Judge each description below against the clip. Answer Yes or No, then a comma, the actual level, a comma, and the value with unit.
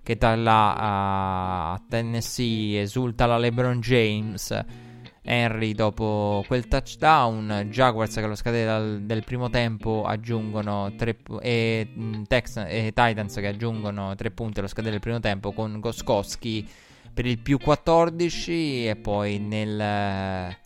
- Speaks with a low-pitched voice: Yes, low, 110 Hz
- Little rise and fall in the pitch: Yes, narrow, 2.3 semitones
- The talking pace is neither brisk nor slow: Yes, average, 135 wpm